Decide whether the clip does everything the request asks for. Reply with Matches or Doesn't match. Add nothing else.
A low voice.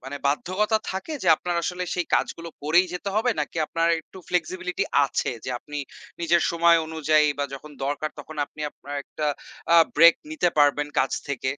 Doesn't match